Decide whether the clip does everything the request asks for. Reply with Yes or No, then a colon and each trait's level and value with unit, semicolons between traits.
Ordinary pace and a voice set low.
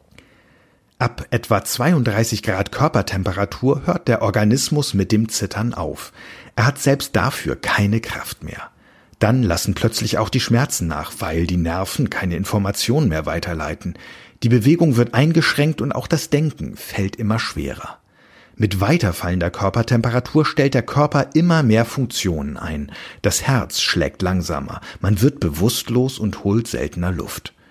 Yes: average, 140 wpm; low, 110 Hz